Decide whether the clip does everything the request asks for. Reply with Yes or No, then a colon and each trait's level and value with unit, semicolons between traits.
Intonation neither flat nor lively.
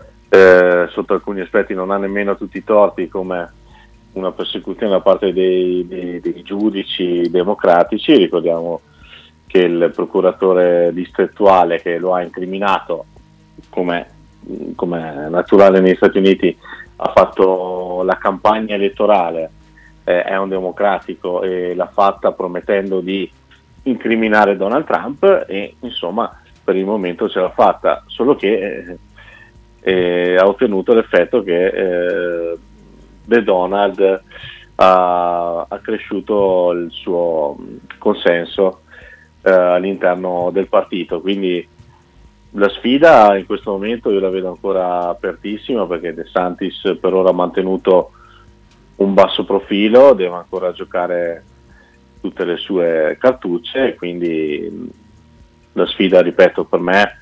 No: narrow, 2.2 semitones